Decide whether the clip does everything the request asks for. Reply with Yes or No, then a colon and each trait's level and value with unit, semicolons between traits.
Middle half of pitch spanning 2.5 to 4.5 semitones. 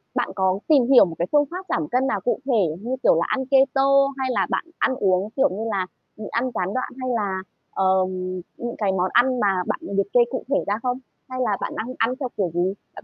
No: average, 5.3 semitones